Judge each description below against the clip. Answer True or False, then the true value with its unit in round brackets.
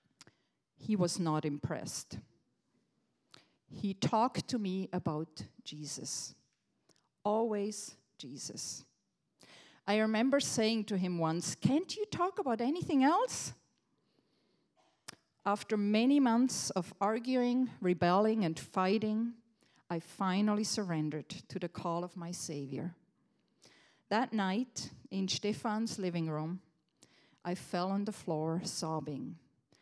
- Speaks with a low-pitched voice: False (195 Hz)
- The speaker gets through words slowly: True (105 wpm)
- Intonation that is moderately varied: True (4.6 semitones)